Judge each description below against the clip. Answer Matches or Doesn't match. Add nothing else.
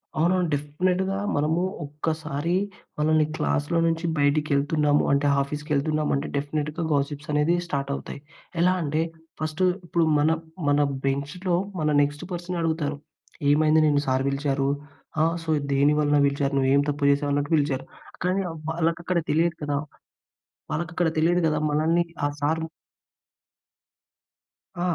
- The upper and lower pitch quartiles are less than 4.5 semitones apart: Matches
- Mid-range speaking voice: Matches